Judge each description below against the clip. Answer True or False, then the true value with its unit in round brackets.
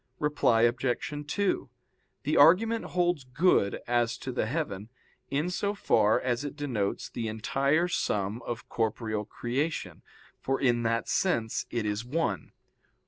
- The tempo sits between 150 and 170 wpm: False (140 wpm)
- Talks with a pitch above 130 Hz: False (125 Hz)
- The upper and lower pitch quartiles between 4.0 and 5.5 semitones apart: True (5.2 semitones)